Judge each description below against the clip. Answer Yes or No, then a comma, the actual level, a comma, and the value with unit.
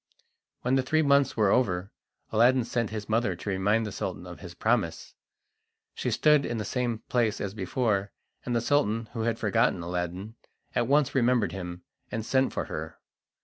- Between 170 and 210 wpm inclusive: Yes, average, 180 wpm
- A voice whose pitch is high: No, low, 115 Hz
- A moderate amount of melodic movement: Yes, average, 4.0 semitones